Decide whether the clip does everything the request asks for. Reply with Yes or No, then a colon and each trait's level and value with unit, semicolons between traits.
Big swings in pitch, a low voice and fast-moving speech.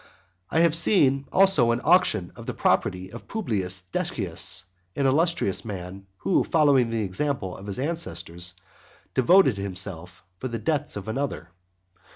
No: wide, 7.9 semitones; low, 115 Hz; average, 145 wpm